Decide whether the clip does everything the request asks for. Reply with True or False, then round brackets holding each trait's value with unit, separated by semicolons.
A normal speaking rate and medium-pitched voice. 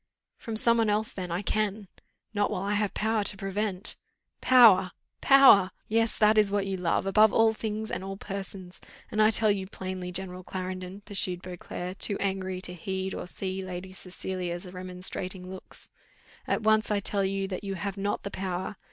False (185 wpm; 195 Hz)